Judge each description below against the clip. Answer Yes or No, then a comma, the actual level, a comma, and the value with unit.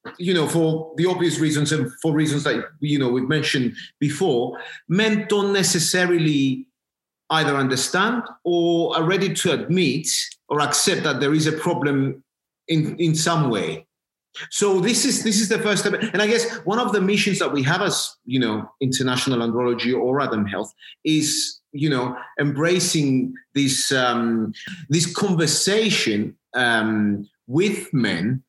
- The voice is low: No, medium, 155 Hz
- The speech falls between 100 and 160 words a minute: Yes, average, 155 wpm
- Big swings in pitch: Yes, wide, 6.0 semitones